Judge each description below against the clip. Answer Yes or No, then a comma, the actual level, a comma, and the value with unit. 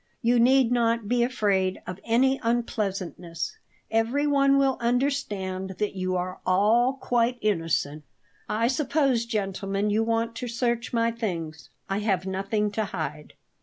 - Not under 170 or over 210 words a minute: No, slow, 135 wpm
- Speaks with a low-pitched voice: No, high, 225 Hz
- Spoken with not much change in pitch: No, average, 4.1 semitones